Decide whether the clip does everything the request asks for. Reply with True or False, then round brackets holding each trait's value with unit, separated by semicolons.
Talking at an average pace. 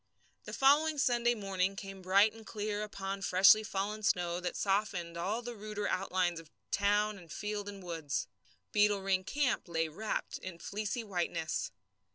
True (160 wpm)